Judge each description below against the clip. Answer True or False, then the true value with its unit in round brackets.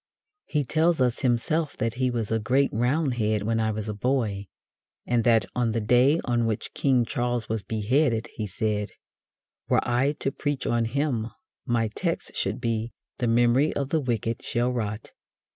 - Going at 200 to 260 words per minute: False (175 wpm)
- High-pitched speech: False (120 Hz)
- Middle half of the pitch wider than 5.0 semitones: False (2.9 semitones)